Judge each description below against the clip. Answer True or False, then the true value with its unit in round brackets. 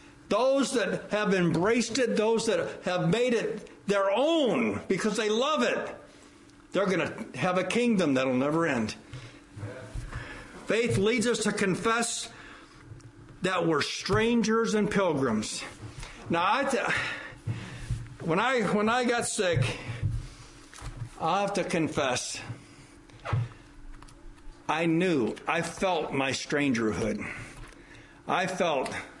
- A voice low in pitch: False (185 Hz)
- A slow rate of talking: True (115 wpm)